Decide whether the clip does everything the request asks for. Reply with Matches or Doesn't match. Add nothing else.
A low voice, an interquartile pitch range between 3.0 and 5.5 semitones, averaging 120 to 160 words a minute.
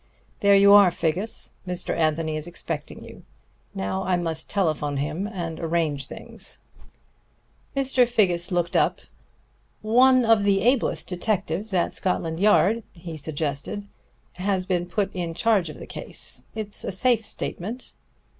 Doesn't match